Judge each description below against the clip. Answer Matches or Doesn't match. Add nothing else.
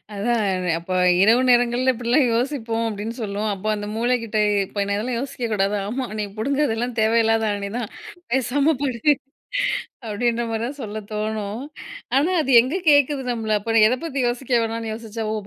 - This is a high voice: Matches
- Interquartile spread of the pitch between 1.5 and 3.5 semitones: Matches